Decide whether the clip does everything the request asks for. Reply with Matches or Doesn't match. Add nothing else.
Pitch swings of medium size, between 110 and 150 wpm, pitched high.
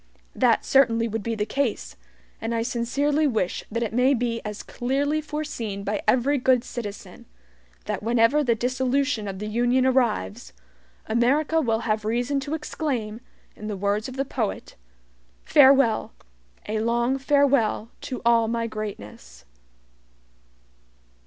Matches